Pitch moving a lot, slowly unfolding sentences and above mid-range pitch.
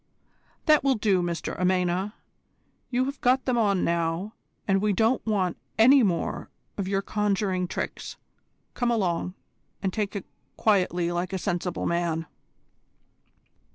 No: average, 3.6 semitones; slow, 130 wpm; high, 195 Hz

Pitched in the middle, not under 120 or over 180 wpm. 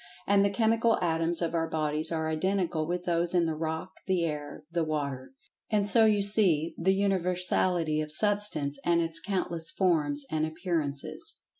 Yes: medium, 170 Hz; average, 165 wpm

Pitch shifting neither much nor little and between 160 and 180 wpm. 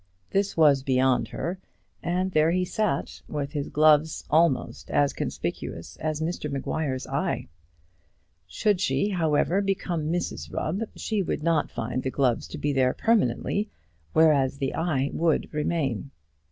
No: average, 4.4 semitones; average, 145 wpm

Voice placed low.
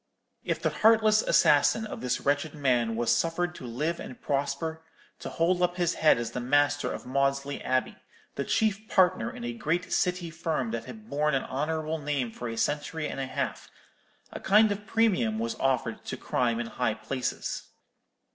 No: medium, 150 Hz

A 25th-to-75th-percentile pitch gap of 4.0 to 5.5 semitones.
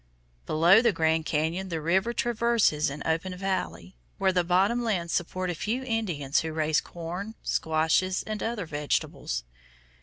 Yes: average, 4.6 semitones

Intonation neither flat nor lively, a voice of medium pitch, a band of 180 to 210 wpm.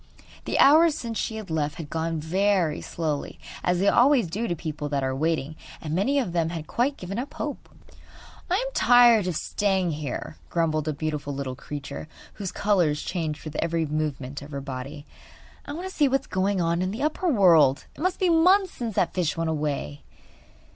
No: wide, 7.4 semitones; medium, 170 Hz; average, 200 wpm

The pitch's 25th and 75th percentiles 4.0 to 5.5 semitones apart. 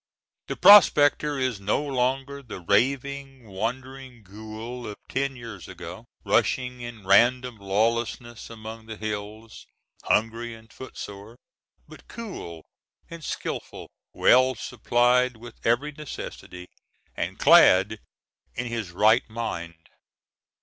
No: average, 3.3 semitones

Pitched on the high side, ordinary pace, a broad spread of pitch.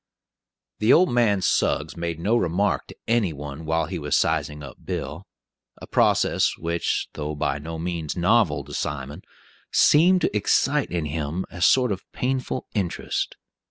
No: very low, 85 Hz; average, 160 wpm; wide, 6.0 semitones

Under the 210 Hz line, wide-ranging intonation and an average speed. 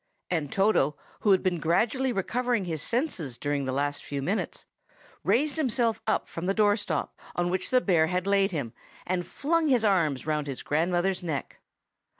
Yes: medium, 185 Hz; wide, 6.2 semitones; average, 165 wpm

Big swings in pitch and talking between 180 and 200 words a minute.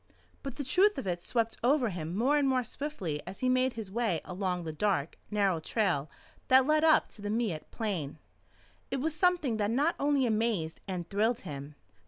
Yes: wide, 6.6 semitones; average, 195 wpm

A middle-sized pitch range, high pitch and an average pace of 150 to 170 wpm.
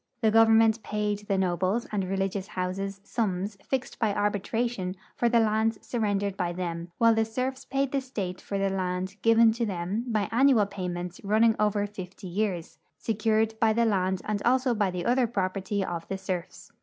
No: average, 3.2 semitones; high, 205 Hz; average, 180 wpm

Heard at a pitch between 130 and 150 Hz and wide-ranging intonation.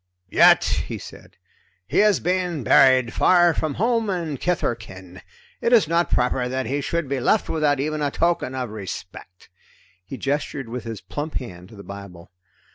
Yes: low, 135 Hz; wide, 6.9 semitones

